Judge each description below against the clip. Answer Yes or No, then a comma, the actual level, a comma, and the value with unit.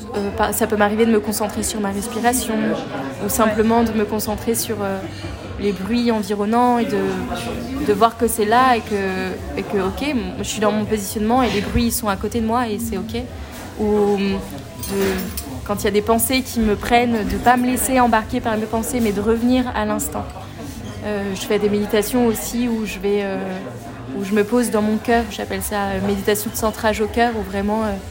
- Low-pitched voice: No, high, 215 Hz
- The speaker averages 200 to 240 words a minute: Yes, average, 215 wpm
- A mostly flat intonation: Yes, narrow, 2.1 semitones